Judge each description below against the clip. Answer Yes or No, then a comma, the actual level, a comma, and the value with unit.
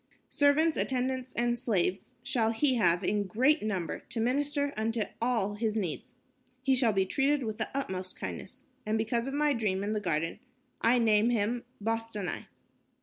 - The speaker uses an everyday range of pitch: Yes, average, 3.8 semitones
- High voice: Yes, high, 225 Hz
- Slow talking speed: No, average, 165 wpm